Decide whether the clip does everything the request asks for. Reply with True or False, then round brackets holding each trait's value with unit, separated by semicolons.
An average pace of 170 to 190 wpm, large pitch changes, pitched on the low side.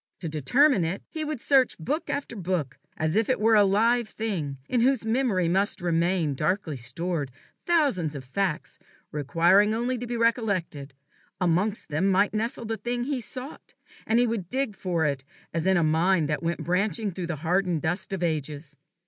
False (180 wpm; 6.0 semitones; 190 Hz)